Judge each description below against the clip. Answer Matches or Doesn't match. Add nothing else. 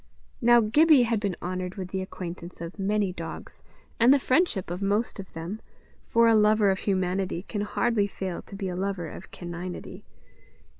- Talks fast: Doesn't match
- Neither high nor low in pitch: Doesn't match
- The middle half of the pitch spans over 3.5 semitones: Doesn't match